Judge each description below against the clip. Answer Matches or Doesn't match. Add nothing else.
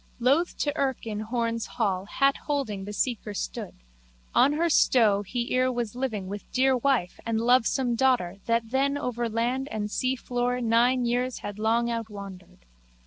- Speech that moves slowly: Doesn't match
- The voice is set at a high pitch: Matches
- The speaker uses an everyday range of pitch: Matches